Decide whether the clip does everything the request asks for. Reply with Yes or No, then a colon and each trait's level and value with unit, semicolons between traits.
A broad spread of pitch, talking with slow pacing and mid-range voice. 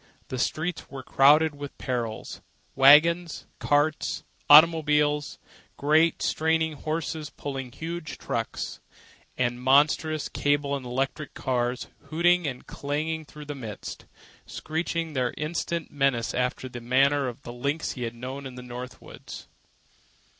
No: average, 3.5 semitones; slow, 125 wpm; medium, 145 Hz